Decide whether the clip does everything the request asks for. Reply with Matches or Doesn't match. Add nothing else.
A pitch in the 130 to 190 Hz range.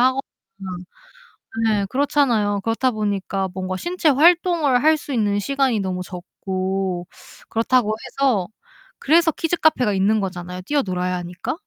Doesn't match